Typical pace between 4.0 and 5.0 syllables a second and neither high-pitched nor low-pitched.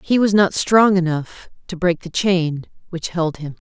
Yes: 4.2 syllables/s; medium, 175 Hz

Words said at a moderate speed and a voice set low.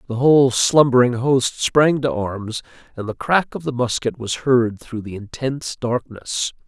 Yes: average, 170 wpm; low, 125 Hz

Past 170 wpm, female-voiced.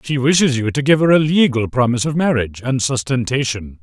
No: fast, 205 wpm; male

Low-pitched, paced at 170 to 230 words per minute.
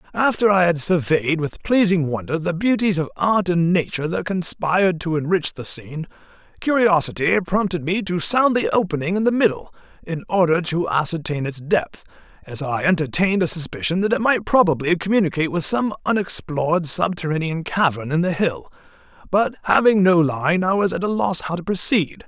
No: medium, 175 Hz; average, 175 wpm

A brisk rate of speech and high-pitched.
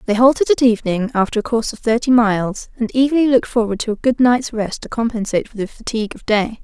Yes: fast, 235 wpm; high, 230 Hz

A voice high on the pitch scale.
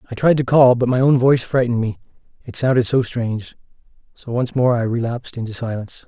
No: low, 120 Hz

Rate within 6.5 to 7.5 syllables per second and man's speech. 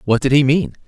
No: 5.9 syllables/s; male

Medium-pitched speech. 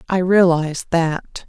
Yes: medium, 175 Hz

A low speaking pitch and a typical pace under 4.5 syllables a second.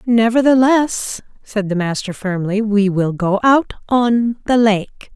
No: high, 220 Hz; 3.7 syllables/s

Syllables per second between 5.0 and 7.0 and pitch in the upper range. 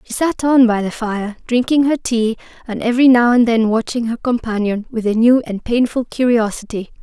Yes: 5.2 syllables/s; high, 235 Hz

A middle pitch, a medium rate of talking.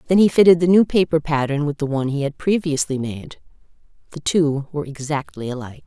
Yes: medium, 150 Hz; average, 185 wpm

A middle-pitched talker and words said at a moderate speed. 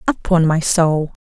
Yes: medium, 165 Hz; average, 145 wpm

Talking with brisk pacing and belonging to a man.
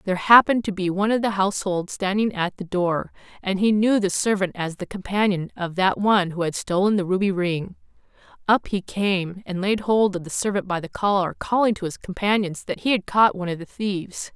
No: fast, 220 wpm; female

